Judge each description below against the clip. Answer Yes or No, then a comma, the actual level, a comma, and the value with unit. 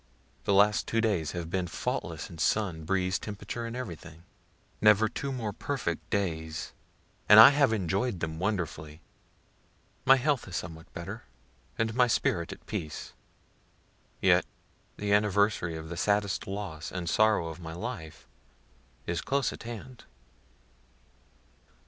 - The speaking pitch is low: Yes, low, 100 Hz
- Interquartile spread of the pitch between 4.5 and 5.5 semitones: Yes, average, 4.9 semitones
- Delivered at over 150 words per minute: No, slow, 135 wpm